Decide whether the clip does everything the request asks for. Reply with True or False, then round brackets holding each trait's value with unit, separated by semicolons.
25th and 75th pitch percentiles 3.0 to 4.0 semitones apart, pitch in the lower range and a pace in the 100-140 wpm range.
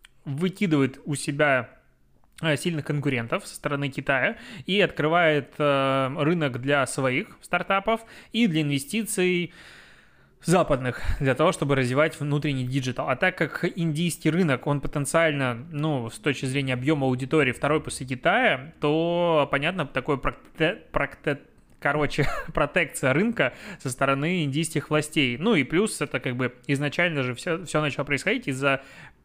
False (3.3 semitones; 150 Hz; 130 wpm)